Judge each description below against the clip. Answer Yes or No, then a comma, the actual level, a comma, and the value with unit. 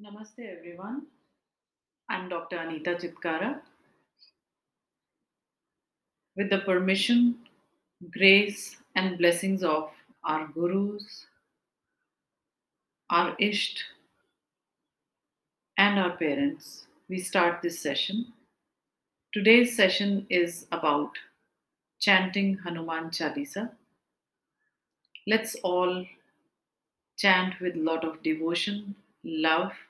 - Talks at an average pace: No, slow, 80 wpm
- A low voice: No, medium, 185 Hz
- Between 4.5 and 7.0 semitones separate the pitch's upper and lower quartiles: No, average, 3.2 semitones